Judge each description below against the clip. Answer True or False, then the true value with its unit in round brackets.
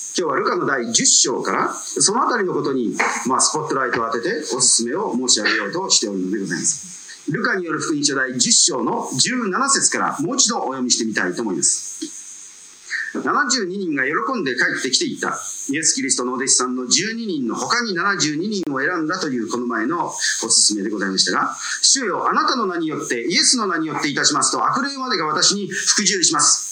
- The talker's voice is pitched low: False (245 Hz)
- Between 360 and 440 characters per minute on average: True (405 characters per minute)